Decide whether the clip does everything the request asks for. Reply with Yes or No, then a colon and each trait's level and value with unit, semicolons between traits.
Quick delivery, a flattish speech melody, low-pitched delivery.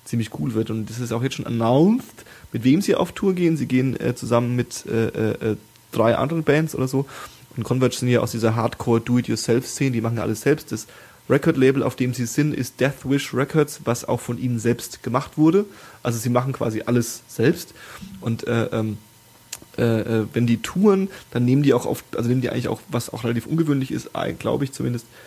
No: fast, 205 wpm; average, 3.0 semitones; low, 125 Hz